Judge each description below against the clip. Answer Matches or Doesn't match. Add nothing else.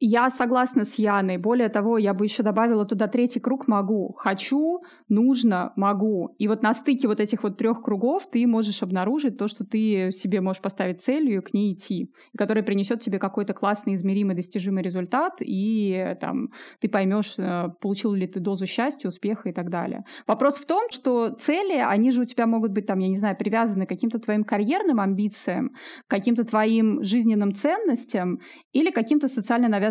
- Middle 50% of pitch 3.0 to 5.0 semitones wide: Matches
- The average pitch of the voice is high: Matches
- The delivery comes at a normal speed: Doesn't match